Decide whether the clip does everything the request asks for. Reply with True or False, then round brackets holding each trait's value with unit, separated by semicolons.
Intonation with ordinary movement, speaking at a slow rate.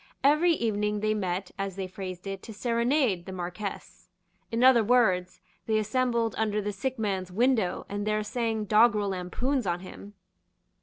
False (3.5 semitones; 160 wpm)